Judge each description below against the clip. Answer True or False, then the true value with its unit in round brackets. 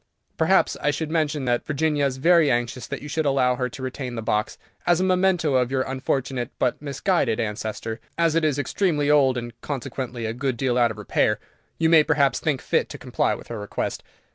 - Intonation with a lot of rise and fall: False (4.0 semitones)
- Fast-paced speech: True (210 wpm)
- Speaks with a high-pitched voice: False (135 Hz)